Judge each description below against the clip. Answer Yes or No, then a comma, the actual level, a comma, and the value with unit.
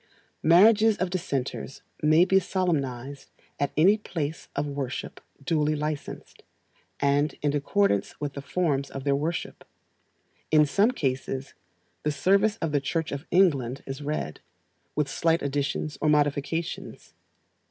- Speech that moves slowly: Yes, slow, 130 wpm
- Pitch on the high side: No, medium, 150 Hz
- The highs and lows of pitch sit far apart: No, average, 3.6 semitones